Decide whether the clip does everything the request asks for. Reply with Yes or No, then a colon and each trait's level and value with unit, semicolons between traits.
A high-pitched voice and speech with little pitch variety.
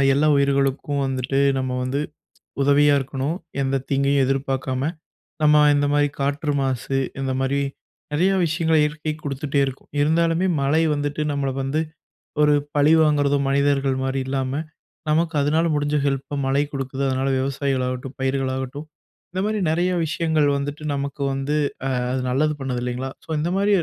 No: medium, 140 Hz; narrow, 2.0 semitones